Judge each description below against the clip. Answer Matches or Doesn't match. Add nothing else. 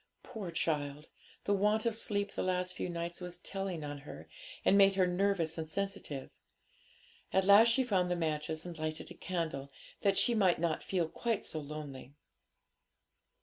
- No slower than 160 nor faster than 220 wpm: Matches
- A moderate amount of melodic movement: Matches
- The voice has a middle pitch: Matches